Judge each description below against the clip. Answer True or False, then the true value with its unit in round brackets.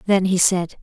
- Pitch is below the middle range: False (185 Hz)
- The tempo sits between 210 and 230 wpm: True (215 wpm)